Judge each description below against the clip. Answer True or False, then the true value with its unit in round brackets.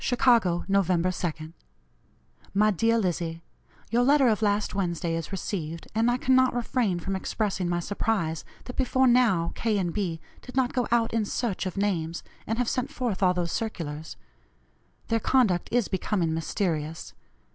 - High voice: True (200 Hz)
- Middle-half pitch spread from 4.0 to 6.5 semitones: True (5.3 semitones)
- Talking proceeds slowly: False (160 wpm)